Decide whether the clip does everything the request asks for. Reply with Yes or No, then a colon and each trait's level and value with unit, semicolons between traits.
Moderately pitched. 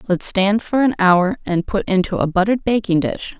No: high, 195 Hz